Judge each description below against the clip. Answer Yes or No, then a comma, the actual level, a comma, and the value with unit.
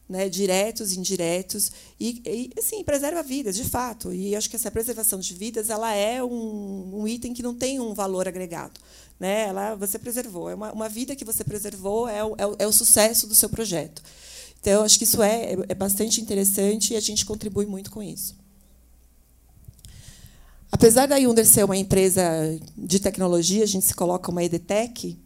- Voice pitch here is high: Yes, high, 210 Hz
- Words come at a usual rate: No, fast, 190 wpm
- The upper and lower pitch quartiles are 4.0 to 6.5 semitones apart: No, average, 3.2 semitones